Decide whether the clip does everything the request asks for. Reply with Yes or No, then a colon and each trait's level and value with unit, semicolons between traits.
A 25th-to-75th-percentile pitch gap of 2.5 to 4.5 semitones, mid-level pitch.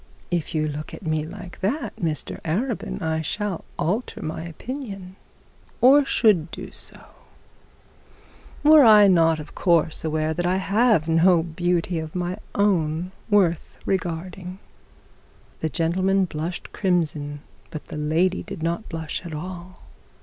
Yes: average, 3.3 semitones; medium, 175 Hz